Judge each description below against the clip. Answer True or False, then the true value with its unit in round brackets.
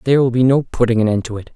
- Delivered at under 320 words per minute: False (345 wpm)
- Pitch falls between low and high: False (120 Hz)